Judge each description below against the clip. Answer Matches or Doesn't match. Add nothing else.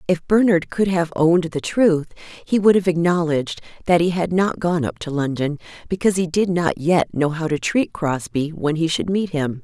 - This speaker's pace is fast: Matches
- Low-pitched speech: Doesn't match